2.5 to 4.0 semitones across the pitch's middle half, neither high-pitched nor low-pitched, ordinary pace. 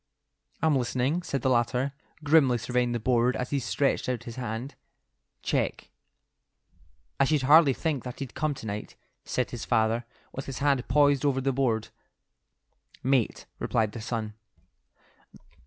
No: average, 2.8 semitones; low, 130 Hz; average, 150 wpm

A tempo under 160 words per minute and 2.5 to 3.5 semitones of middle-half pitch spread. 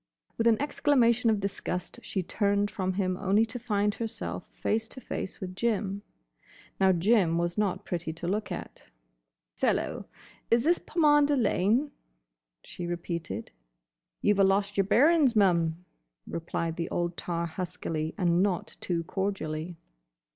No: average, 145 wpm; average, 4.4 semitones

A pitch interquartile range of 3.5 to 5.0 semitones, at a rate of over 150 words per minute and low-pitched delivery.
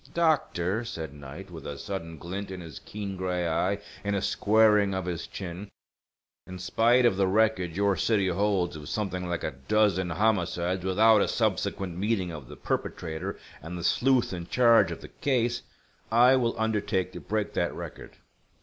Yes: average, 3.8 semitones; average, 175 wpm; very low, 95 Hz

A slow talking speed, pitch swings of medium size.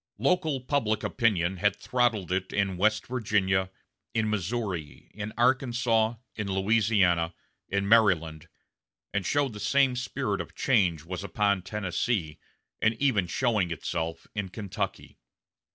Yes: slow, 120 wpm; average, 3.8 semitones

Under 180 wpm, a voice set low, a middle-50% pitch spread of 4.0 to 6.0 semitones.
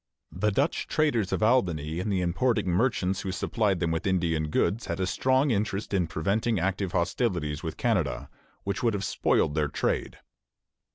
Yes: average, 170 wpm; very low, 95 Hz; average, 4.3 semitones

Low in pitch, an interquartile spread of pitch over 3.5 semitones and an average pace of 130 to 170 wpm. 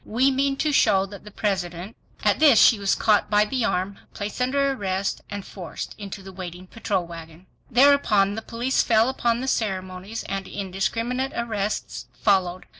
No: high, 205 Hz; average, 3.9 semitones; average, 165 wpm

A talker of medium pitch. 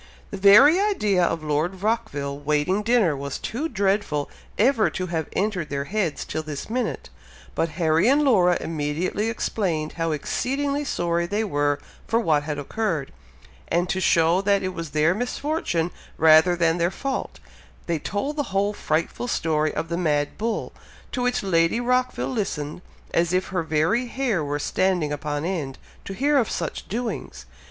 Yes: medium, 180 Hz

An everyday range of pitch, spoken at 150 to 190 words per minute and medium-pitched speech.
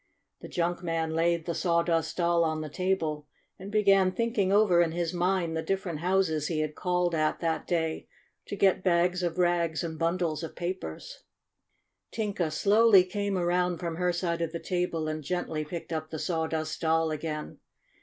No: narrow, 2.1 semitones; average, 175 wpm; medium, 170 Hz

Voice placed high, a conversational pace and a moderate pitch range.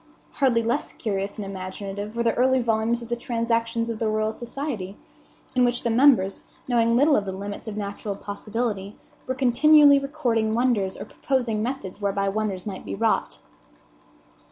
Yes: high, 230 Hz; average, 165 wpm; average, 3.3 semitones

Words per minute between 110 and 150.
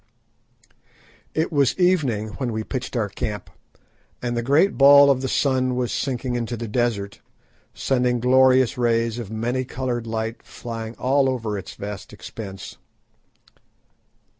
Yes: average, 140 wpm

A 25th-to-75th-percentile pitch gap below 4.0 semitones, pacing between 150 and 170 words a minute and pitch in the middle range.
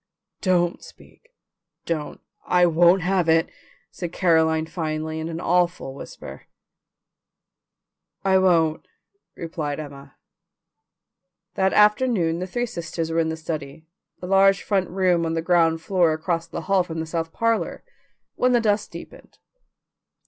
No: average, 2.7 semitones; slow, 135 wpm; medium, 170 Hz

